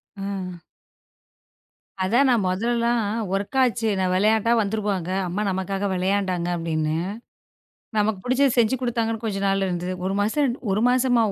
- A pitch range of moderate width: Yes, average, 3.8 semitones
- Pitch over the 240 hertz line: No, high, 205 Hz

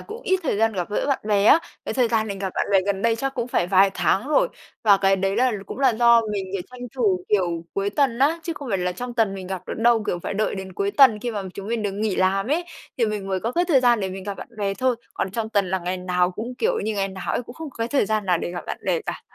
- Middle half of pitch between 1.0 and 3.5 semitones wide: No, average, 4.1 semitones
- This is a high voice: Yes, high, 210 Hz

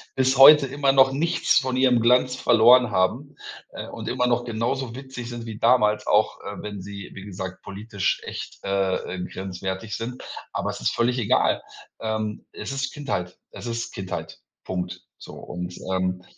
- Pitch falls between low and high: No, low, 115 Hz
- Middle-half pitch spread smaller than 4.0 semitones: No, average, 4.7 semitones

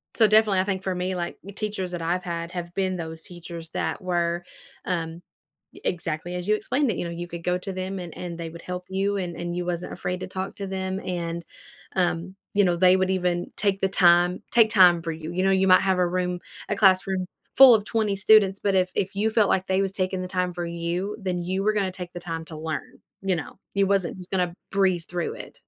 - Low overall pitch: No, medium, 185 Hz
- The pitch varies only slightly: Yes, narrow, 1.8 semitones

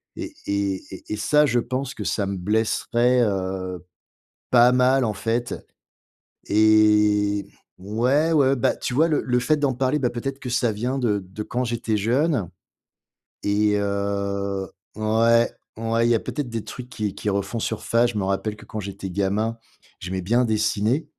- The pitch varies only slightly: No, average, 3.5 semitones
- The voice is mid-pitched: No, low, 110 Hz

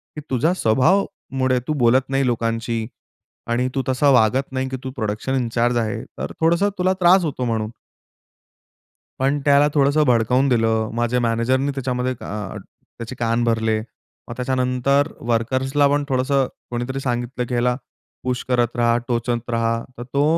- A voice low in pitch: Yes, low, 125 Hz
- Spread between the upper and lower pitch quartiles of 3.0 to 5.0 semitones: No, narrow, 2.5 semitones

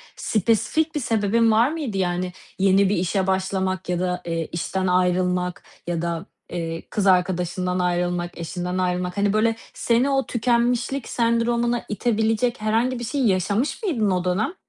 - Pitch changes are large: No, average, 4.5 semitones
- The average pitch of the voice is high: Yes, high, 195 Hz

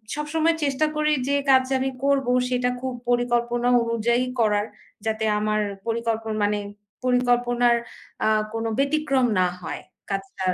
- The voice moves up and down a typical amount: Yes, average, 3.0 semitones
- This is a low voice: No, high, 240 Hz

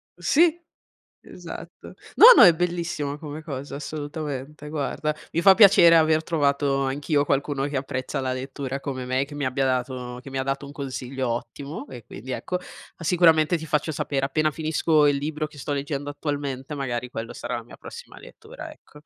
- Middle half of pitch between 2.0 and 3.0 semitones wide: Yes, average, 2.7 semitones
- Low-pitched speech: No, medium, 145 Hz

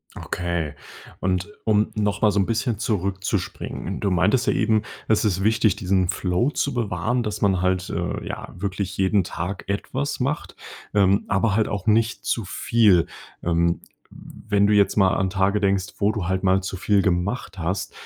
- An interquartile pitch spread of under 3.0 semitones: Yes, narrow, 2.5 semitones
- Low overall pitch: Yes, low, 100 Hz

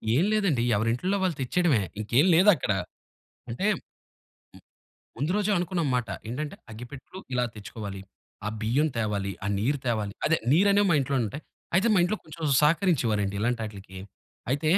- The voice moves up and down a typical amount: No, wide, 8.0 semitones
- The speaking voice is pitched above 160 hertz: No, low, 135 Hz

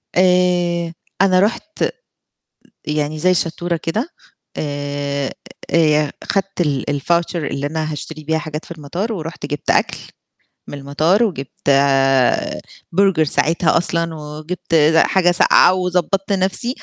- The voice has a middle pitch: Yes, medium, 165 Hz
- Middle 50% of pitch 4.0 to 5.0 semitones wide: No, average, 3.3 semitones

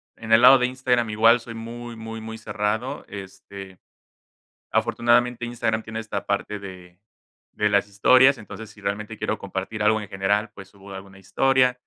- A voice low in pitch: Yes, low, 110 Hz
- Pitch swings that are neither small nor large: Yes, average, 3.0 semitones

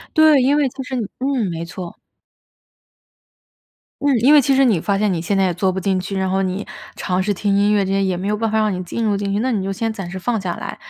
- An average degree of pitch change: Yes, average, 3.7 semitones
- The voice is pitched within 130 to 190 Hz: No, high, 200 Hz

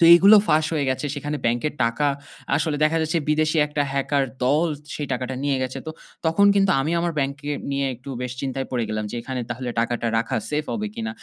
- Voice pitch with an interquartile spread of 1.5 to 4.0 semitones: Yes, average, 3.4 semitones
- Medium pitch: Yes, medium, 145 Hz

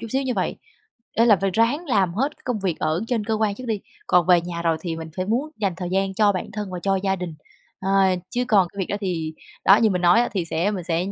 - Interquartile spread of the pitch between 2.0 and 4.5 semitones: Yes, average, 3.8 semitones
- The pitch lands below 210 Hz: Yes, high, 195 Hz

